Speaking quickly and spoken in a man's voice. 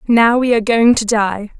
No: fast, 225 wpm; female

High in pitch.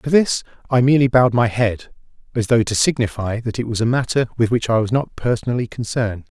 No: low, 120 Hz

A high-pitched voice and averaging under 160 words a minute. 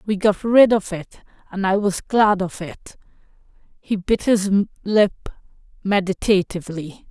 Yes: high, 195 Hz; slow, 135 wpm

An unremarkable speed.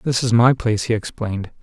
No: fast, 220 wpm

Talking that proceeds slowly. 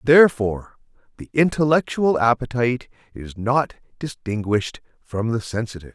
Yes: slow, 100 wpm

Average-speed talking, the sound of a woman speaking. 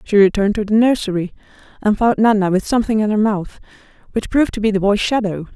No: fast, 215 wpm; female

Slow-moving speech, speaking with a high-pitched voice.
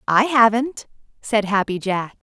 Yes: slow, 130 wpm; high, 220 Hz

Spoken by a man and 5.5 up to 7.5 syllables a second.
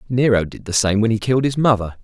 Yes: male; 6.5 syllables/s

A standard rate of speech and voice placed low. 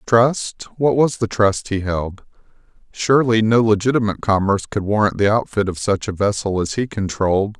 Yes: average, 165 wpm; low, 105 Hz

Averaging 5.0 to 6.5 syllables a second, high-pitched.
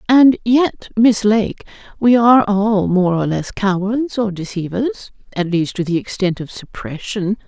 No: 4.2 syllables/s; high, 205 Hz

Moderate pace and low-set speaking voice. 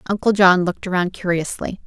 No: average, 160 wpm; medium, 185 Hz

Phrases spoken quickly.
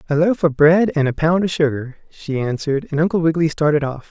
Yes: fast, 235 wpm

